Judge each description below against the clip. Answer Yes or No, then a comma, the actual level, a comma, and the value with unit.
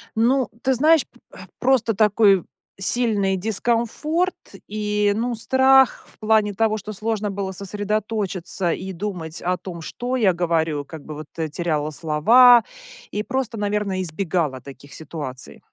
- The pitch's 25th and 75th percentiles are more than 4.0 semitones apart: Yes, average, 4.9 semitones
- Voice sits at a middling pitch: No, high, 205 Hz